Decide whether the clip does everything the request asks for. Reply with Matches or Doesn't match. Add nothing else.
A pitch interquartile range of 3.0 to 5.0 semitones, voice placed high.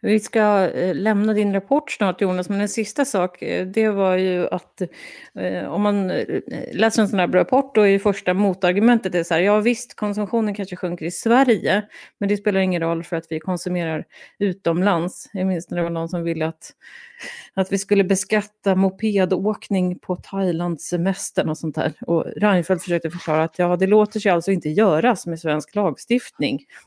Matches